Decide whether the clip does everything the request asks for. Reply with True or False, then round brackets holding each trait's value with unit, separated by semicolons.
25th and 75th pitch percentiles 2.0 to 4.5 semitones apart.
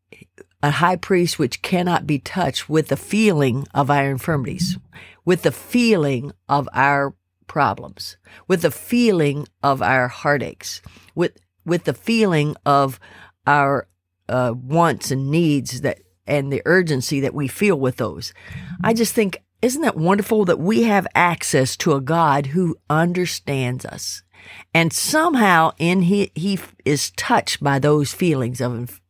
False (5.2 semitones)